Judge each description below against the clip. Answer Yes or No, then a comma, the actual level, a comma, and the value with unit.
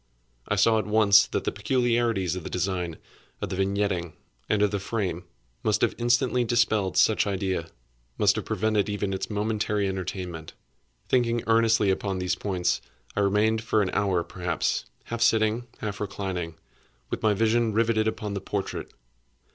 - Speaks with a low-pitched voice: Yes, low, 105 Hz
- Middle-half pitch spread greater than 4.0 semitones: No, average, 2.9 semitones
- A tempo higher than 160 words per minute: No, average, 155 wpm